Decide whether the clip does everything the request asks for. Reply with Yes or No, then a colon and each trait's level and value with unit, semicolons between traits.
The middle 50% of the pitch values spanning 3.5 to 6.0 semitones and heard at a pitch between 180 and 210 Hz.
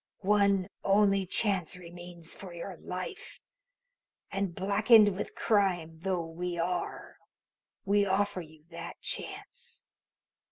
No: narrow, 2.6 semitones; high, 190 Hz